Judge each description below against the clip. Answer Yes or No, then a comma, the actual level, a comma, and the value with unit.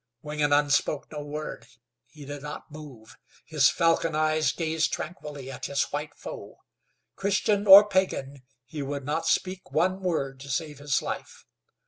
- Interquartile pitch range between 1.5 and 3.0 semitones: Yes, average, 2.7 semitones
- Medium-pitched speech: Yes, medium, 150 Hz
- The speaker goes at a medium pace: Yes, average, 150 wpm